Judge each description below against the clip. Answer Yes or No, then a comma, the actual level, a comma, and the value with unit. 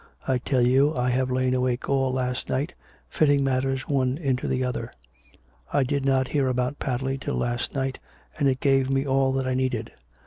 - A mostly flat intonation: Yes, narrow, 1.1 semitones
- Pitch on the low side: Yes, low, 130 Hz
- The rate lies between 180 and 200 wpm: Yes, average, 195 wpm